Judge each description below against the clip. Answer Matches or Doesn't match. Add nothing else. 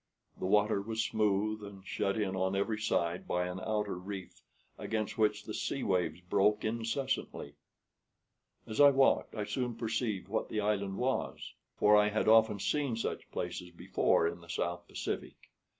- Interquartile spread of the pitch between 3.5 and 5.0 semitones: Doesn't match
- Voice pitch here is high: Doesn't match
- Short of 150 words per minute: Doesn't match